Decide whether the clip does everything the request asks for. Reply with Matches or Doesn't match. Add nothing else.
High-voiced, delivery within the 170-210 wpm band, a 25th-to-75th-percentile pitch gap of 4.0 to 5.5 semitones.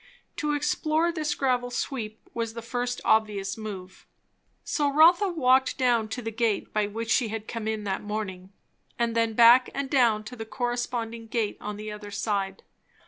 Doesn't match